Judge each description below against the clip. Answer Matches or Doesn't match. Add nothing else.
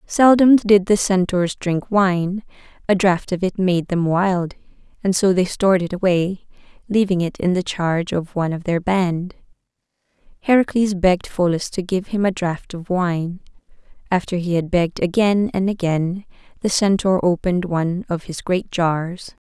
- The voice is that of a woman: Matches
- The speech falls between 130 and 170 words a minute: Matches